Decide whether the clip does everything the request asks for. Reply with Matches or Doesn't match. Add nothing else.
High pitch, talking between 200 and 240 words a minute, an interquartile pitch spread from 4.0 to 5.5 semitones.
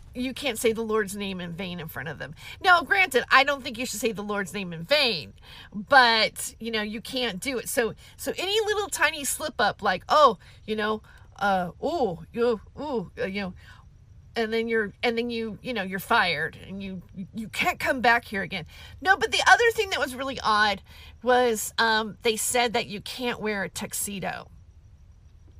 Matches